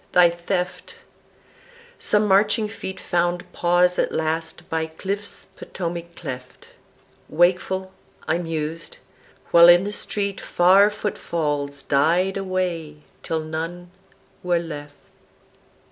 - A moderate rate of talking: No, slow, 105 wpm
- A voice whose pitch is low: No, medium, 175 Hz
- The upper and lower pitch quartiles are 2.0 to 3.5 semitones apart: Yes, average, 2.7 semitones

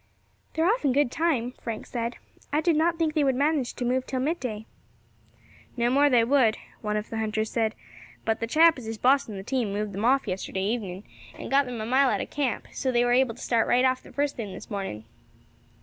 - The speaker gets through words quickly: Yes, fast, 235 wpm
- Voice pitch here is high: Yes, high, 245 Hz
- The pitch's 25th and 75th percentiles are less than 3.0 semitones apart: No, average, 4.1 semitones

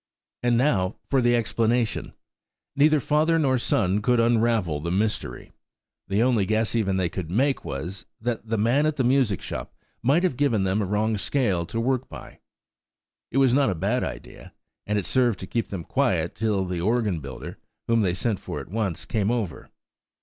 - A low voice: Yes, low, 110 Hz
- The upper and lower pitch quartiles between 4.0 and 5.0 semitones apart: Yes, average, 4.6 semitones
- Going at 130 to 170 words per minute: No, average, 190 wpm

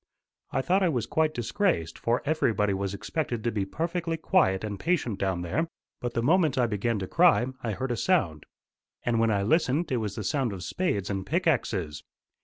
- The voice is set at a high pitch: No, low, 120 Hz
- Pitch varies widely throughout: Yes, wide, 8.1 semitones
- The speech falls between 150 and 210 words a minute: Yes, average, 200 wpm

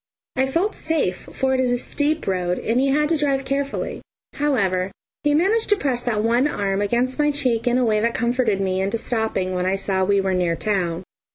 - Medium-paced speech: No, fast, 215 wpm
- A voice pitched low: No, high, 235 Hz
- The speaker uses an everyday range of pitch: No, wide, 6.1 semitones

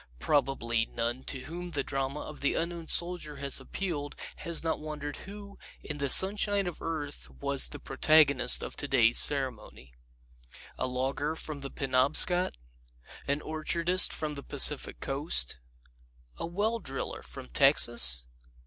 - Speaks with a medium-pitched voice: Yes, medium, 145 Hz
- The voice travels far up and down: No, average, 4.2 semitones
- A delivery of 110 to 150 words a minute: Yes, average, 140 wpm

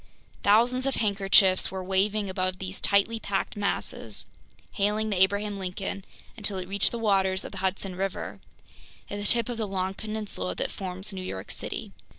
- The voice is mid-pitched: No, high, 195 Hz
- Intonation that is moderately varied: No, narrow, 1.9 semitones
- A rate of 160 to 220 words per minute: Yes, average, 170 wpm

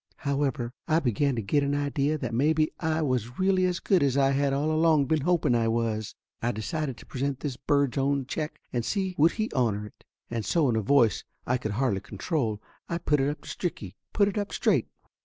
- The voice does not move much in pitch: No, average, 4.6 semitones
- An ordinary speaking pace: No, fast, 220 wpm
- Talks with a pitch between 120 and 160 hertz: Yes, medium, 140 Hz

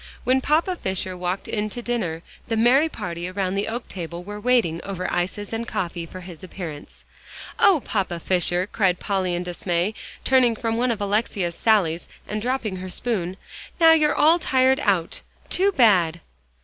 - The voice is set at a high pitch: Yes, high, 200 Hz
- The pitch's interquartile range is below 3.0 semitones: No, average, 5.2 semitones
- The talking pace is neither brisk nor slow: Yes, average, 175 wpm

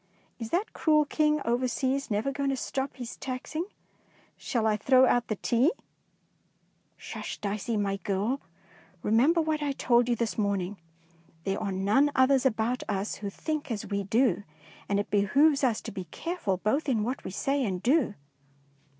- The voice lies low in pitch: No, high, 240 Hz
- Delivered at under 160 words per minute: No, average, 175 wpm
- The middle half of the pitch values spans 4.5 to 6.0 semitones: Yes, average, 5.1 semitones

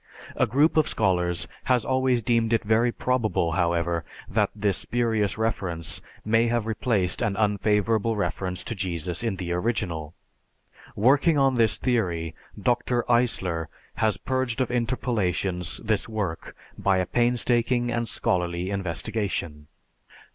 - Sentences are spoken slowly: Yes, slow, 130 wpm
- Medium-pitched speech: No, low, 110 Hz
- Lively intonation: No, average, 4.9 semitones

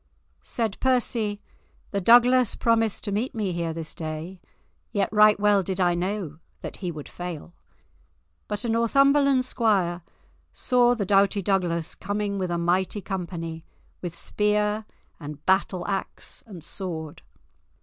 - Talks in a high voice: Yes, high, 195 Hz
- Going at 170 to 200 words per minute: No, average, 140 wpm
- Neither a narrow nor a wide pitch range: Yes, average, 3.8 semitones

